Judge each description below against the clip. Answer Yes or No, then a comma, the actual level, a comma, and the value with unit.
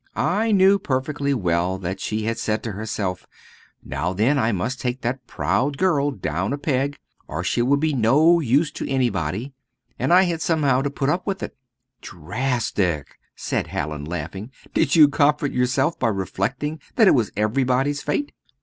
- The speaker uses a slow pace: No, average, 170 wpm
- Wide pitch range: Yes, wide, 6.4 semitones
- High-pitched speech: No, low, 130 Hz